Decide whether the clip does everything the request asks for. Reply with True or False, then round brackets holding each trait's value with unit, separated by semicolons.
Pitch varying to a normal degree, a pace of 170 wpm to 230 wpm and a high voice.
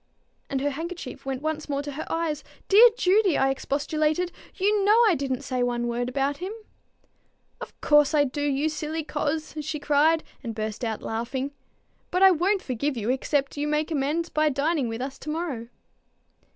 True (3.3 semitones; 180 wpm; 290 Hz)